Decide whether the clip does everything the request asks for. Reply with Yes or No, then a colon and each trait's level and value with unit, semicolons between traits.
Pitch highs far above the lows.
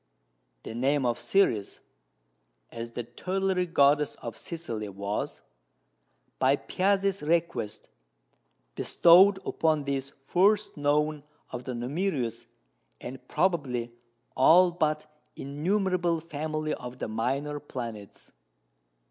Yes: wide, 5.8 semitones